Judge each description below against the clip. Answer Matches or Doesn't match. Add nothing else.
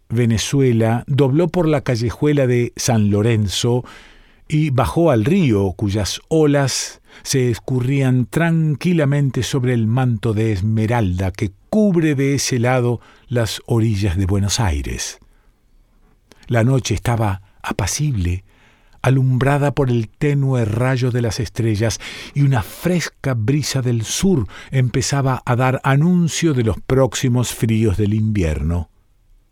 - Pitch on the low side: Matches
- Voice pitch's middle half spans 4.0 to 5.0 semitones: Matches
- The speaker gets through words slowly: Matches